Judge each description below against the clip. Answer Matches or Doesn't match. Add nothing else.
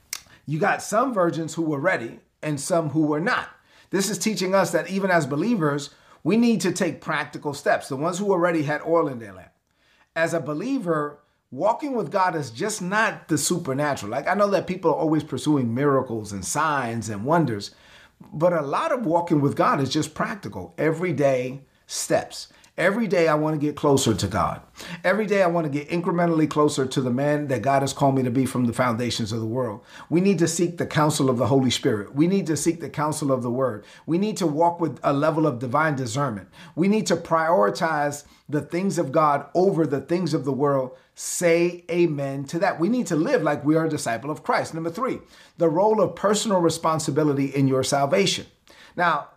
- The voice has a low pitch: Doesn't match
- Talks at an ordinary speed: Doesn't match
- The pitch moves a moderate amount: Matches